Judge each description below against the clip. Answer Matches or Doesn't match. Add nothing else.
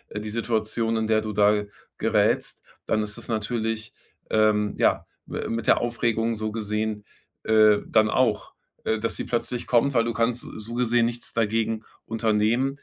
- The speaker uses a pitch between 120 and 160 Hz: Doesn't match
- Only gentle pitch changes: Matches